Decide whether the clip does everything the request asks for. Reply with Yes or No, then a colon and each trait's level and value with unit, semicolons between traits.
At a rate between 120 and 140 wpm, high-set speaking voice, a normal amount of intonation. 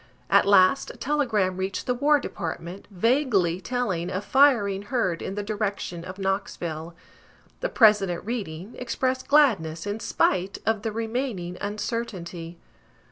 Yes: slow, 135 wpm; high, 200 Hz; average, 4.7 semitones